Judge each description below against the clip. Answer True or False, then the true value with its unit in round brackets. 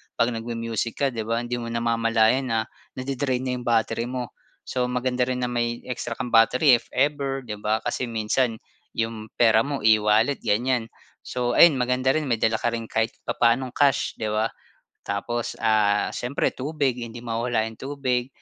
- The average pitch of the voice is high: False (120 Hz)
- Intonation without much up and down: True (2.1 semitones)